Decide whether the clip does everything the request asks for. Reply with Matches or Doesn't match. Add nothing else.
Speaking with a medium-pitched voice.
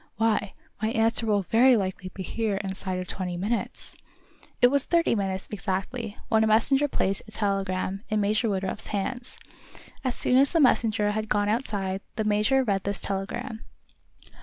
Doesn't match